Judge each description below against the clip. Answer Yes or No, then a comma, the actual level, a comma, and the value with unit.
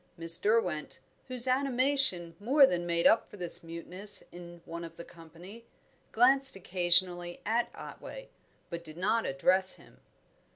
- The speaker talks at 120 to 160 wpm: Yes, average, 140 wpm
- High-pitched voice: No, medium, 180 Hz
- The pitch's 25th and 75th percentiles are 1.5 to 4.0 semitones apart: No, wide, 5.6 semitones